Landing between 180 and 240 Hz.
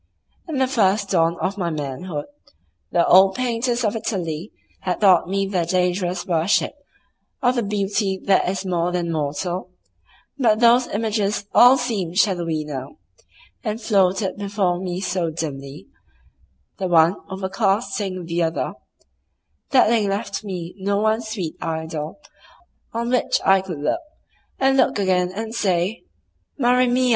Yes: high, 190 Hz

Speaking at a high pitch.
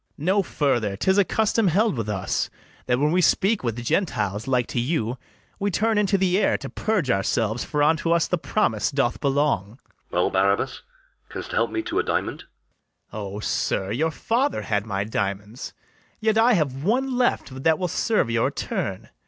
No: medium, 145 Hz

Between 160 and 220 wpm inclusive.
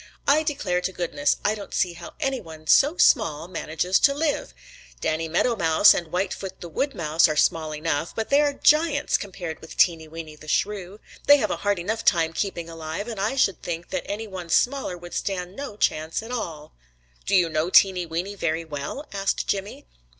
Yes: average, 200 wpm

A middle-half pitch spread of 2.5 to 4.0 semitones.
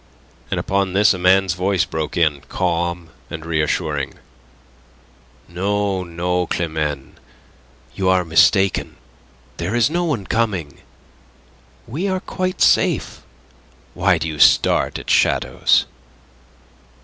Yes: average, 3.3 semitones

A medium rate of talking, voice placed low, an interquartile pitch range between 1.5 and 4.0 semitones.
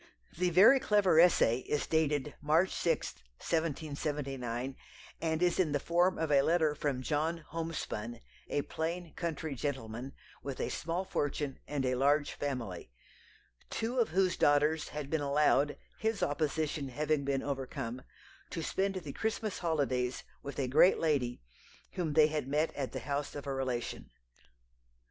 No: average, 150 wpm; medium, 150 Hz; average, 3.2 semitones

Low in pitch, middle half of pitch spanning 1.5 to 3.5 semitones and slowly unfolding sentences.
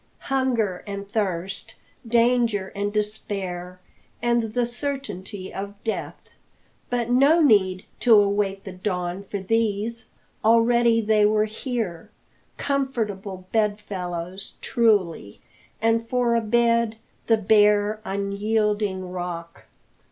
No: high, 210 Hz; average, 3.2 semitones; slow, 105 wpm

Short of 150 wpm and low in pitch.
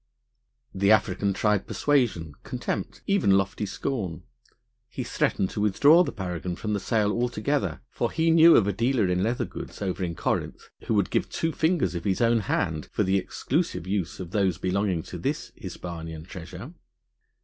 No: average, 170 wpm; low, 100 Hz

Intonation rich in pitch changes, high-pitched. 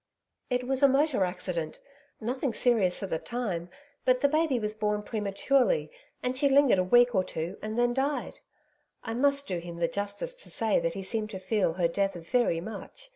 Yes: wide, 5.8 semitones; high, 220 Hz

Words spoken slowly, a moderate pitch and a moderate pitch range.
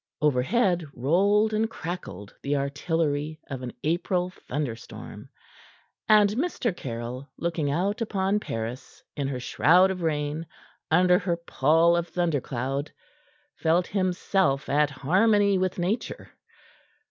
Yes: slow, 115 wpm; medium, 165 Hz; average, 5.0 semitones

